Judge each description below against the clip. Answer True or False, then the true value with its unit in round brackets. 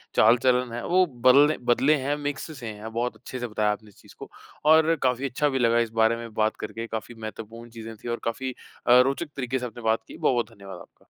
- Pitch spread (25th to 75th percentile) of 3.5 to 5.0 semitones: False (2.8 semitones)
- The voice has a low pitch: True (120 Hz)